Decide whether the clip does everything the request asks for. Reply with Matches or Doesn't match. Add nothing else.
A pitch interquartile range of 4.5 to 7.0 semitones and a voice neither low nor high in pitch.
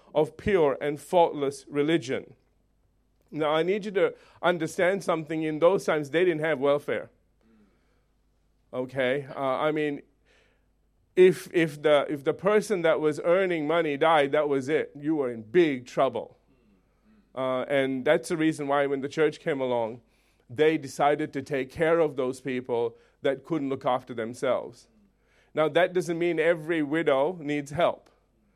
Doesn't match